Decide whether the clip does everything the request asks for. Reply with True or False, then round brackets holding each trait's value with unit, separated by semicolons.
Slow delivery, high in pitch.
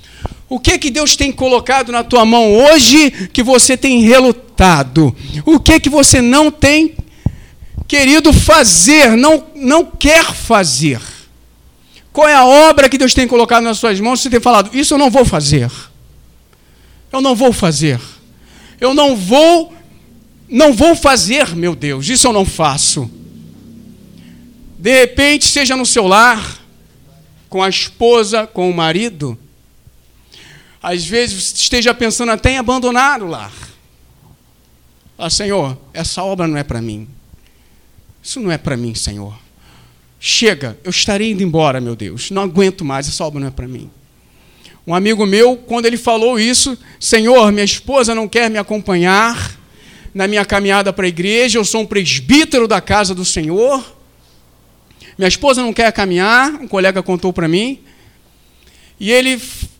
False (155 wpm; 210 Hz)